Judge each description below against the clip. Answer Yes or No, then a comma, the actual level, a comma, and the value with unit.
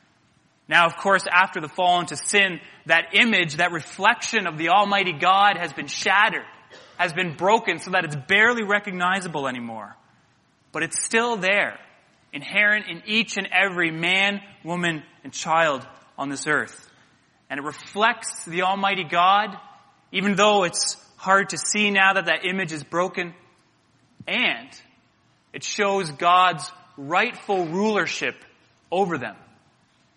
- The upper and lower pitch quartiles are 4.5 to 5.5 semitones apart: No, average, 3.1 semitones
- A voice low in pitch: No, medium, 180 Hz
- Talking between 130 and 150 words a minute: Yes, average, 140 wpm